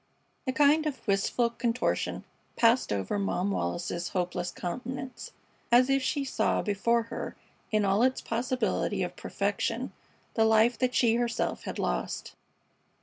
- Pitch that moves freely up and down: No, average, 4.3 semitones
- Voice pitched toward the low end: No, high, 230 Hz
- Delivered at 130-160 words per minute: Yes, average, 140 wpm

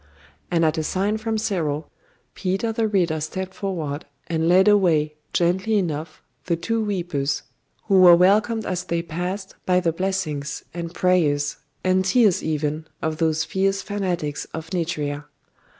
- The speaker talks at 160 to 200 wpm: No, average, 150 wpm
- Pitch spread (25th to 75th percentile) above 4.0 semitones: No, average, 3.4 semitones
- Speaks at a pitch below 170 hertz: No, medium, 175 Hz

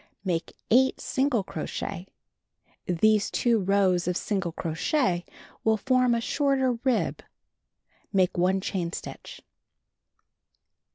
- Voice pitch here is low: No, high, 200 Hz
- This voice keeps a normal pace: No, slow, 100 wpm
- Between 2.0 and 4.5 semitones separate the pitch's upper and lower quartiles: No, average, 5.2 semitones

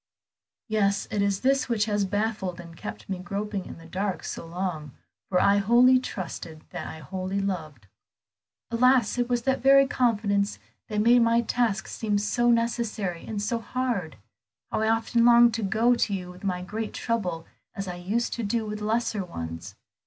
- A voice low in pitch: No, high, 210 Hz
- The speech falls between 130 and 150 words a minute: No, average, 180 wpm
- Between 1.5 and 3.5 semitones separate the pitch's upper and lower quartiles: No, average, 4.0 semitones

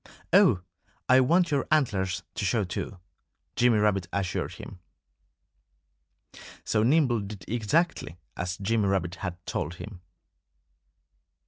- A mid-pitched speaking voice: No, low, 105 Hz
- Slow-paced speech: Yes, slow, 115 wpm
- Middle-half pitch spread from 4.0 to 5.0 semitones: Yes, average, 4.7 semitones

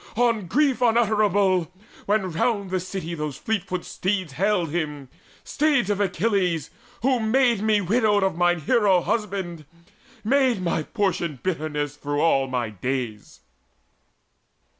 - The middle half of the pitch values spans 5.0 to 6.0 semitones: Yes, average, 5.3 semitones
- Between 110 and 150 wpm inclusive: Yes, slow, 135 wpm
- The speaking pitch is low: No, high, 190 Hz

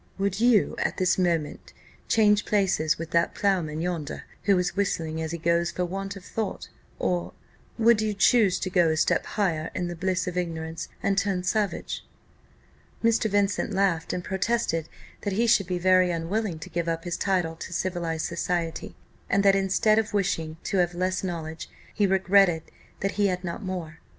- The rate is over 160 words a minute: Yes, average, 180 wpm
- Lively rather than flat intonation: No, average, 2.9 semitones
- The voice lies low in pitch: No, medium, 185 Hz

